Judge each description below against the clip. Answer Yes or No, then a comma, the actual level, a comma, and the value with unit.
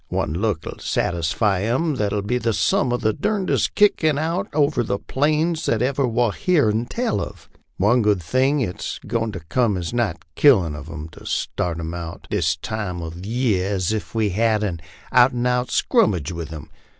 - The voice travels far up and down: Yes, wide, 6.5 semitones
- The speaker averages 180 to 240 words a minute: Yes, average, 190 wpm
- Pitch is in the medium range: No, low, 110 Hz